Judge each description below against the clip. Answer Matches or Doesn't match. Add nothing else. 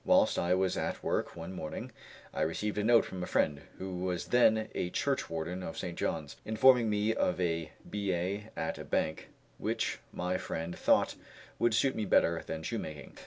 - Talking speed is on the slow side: Doesn't match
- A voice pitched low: Matches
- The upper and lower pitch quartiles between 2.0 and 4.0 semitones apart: Doesn't match